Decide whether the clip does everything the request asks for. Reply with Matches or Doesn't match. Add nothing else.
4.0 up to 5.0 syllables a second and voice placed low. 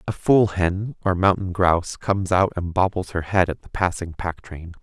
Matches